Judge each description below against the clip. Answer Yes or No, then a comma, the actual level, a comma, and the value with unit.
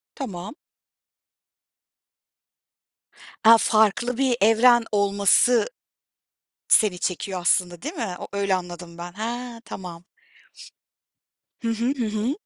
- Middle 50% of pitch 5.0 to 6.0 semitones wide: No, average, 4.6 semitones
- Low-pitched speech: No, high, 215 Hz